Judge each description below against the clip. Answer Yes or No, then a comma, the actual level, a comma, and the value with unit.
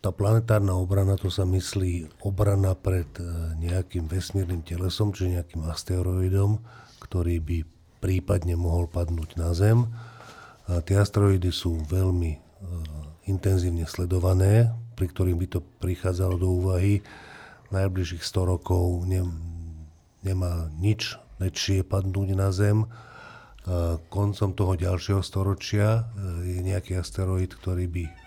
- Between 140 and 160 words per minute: No, slow, 110 wpm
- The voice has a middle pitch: No, very low, 95 Hz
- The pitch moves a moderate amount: No, narrow, 2.2 semitones